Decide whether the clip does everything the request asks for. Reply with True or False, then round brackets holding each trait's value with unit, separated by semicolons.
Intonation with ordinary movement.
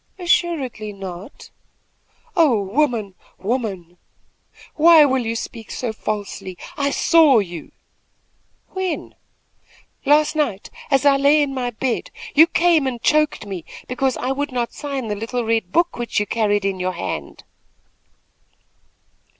False (6.0 semitones)